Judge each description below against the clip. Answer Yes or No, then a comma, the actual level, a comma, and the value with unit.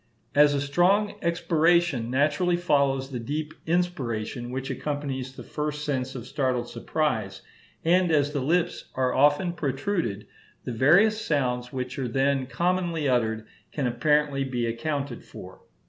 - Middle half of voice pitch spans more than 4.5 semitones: No, average, 4.2 semitones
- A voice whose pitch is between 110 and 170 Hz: Yes, medium, 140 Hz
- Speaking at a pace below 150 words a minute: Yes, average, 140 wpm